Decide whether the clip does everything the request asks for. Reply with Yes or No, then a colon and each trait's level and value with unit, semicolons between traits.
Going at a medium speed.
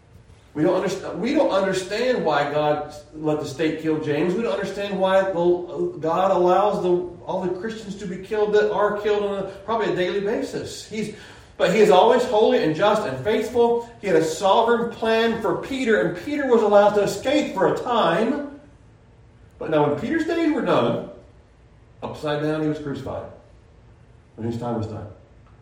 Yes: average, 185 wpm